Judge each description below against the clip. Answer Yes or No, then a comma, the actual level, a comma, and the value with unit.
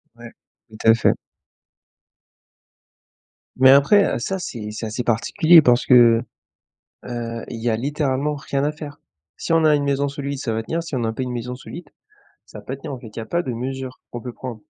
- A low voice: Yes, low, 130 Hz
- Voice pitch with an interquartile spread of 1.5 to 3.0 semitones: No, average, 3.6 semitones